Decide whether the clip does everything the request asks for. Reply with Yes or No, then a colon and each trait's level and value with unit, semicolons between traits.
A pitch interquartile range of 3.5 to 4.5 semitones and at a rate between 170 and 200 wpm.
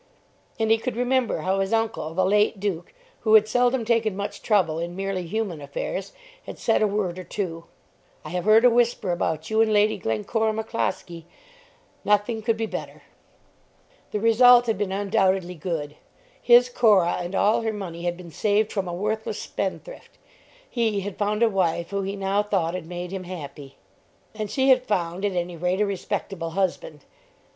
Yes: average, 3.8 semitones; average, 180 wpm